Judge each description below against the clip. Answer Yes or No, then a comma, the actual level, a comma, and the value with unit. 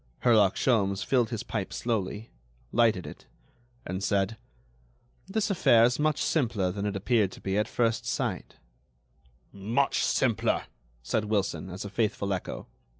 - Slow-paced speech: No, average, 145 wpm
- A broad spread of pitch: No, average, 3.4 semitones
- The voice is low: Yes, low, 110 Hz